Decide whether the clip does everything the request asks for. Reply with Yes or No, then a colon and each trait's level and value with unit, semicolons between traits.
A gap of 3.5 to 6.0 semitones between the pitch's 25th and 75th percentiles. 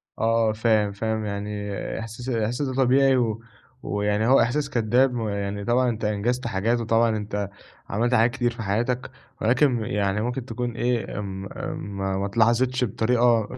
No: average, 2.9 semitones